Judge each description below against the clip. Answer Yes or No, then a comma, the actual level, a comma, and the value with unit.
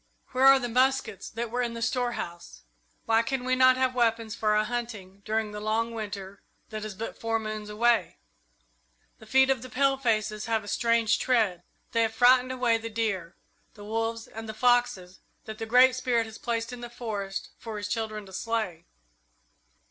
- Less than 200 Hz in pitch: No, high, 225 Hz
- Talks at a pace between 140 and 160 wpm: No, average, 185 wpm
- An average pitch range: No, narrow, 2.3 semitones